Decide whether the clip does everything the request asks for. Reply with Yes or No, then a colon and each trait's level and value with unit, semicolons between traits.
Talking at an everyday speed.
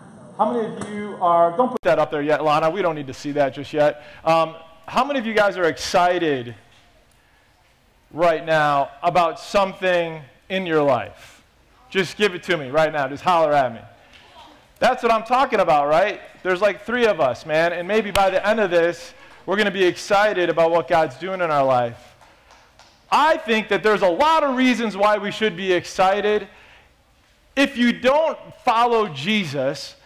Yes: average, 190 wpm